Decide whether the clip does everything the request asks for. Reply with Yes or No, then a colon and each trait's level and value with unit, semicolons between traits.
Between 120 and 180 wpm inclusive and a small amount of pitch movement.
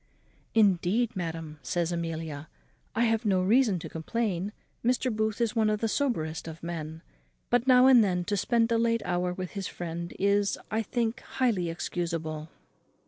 No: average, 165 wpm; average, 5.3 semitones